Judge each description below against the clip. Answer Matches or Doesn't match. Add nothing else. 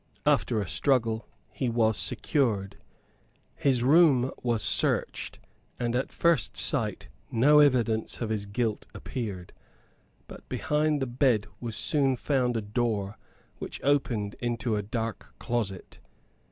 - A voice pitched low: Matches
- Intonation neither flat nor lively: Matches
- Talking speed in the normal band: Doesn't match